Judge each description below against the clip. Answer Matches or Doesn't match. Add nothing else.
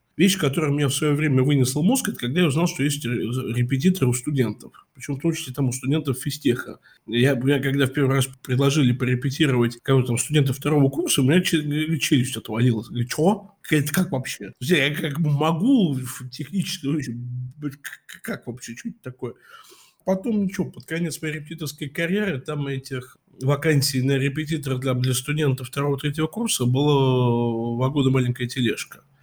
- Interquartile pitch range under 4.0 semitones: Matches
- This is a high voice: Doesn't match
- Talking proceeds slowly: Doesn't match